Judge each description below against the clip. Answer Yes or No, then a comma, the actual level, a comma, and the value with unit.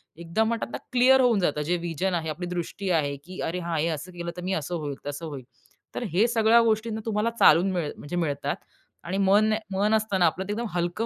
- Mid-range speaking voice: Yes, medium, 180 Hz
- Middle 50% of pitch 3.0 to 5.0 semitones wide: Yes, average, 4.6 semitones